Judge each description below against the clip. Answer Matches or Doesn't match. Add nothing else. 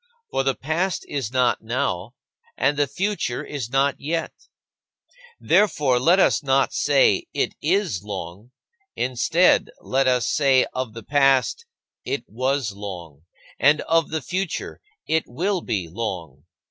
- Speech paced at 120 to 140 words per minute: Matches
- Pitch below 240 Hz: Matches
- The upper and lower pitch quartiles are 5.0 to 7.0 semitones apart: Matches